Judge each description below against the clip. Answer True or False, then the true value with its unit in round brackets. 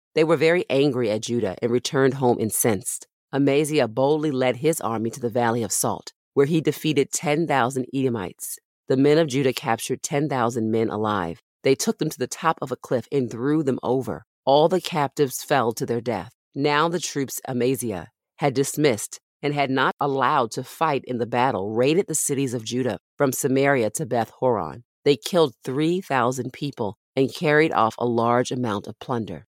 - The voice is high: False (135 Hz)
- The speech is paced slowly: False (190 wpm)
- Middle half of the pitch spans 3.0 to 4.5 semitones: True (3.6 semitones)